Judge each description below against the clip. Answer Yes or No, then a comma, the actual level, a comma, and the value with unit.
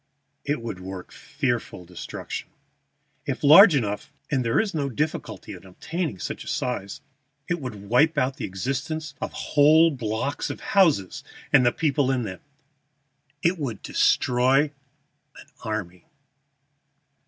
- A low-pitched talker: Yes, low, 130 Hz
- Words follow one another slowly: Yes, slow, 130 wpm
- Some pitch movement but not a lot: No, wide, 6.0 semitones